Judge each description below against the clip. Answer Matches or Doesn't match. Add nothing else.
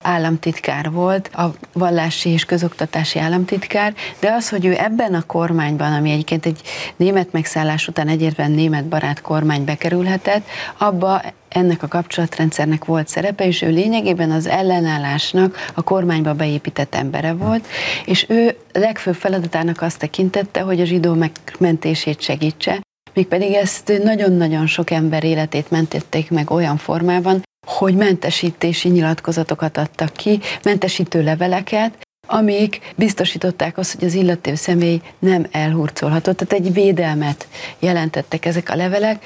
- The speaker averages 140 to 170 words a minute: Doesn't match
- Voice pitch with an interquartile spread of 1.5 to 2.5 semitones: Doesn't match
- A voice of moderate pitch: Matches